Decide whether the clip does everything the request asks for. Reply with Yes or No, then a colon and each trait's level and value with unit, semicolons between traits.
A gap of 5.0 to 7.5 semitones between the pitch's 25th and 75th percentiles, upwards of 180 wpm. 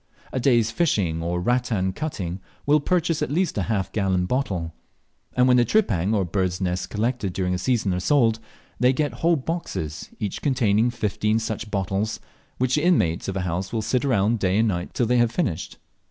Yes: wide, 5.4 semitones; average, 195 wpm